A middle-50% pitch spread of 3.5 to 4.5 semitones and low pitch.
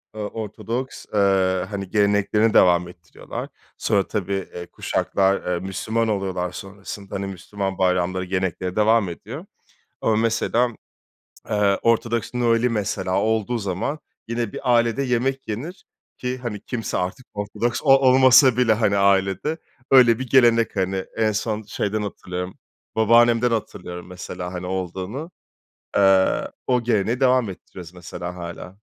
Yes: average, 3.8 semitones; low, 105 Hz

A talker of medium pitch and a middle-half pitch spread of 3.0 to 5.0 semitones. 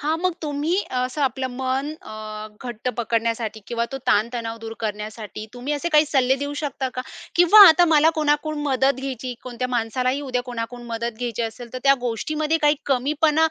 No: very high, 255 Hz; average, 4.0 semitones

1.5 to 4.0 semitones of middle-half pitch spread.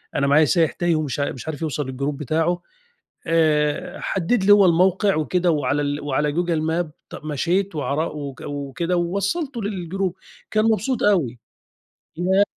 No: average, 4.4 semitones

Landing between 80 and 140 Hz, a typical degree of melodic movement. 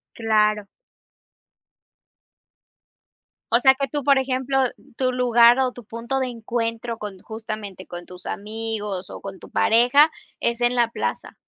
No: high, 235 Hz; average, 3.0 semitones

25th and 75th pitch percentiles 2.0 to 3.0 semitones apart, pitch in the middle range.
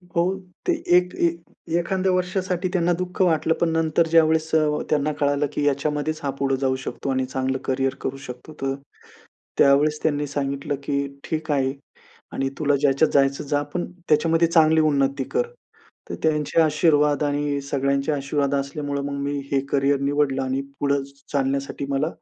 Yes: narrow, 2.5 semitones; medium, 145 Hz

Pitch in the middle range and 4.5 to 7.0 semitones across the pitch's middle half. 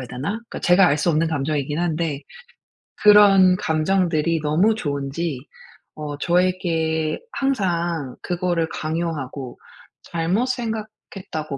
No: medium, 165 Hz; average, 3.4 semitones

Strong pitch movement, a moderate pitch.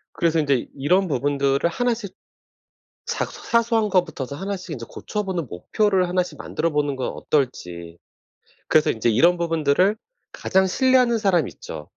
Yes: wide, 5.9 semitones; medium, 170 Hz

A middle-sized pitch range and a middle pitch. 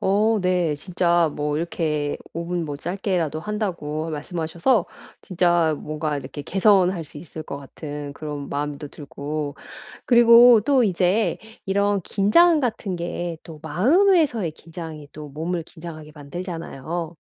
Yes: average, 4.3 semitones; medium, 170 Hz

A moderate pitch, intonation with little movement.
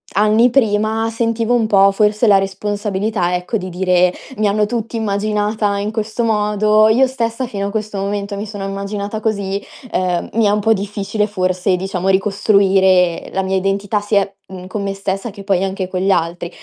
No: high, 205 Hz; narrow, 1.9 semitones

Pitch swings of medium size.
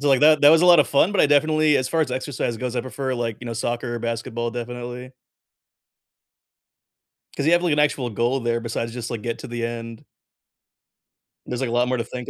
Yes: average, 3.4 semitones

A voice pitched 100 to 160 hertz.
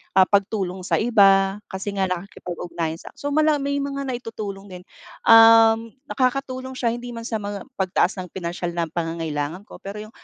No: high, 200 Hz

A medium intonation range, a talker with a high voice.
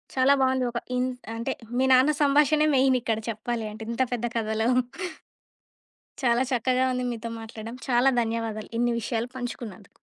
No: narrow, 2.3 semitones; high, 240 Hz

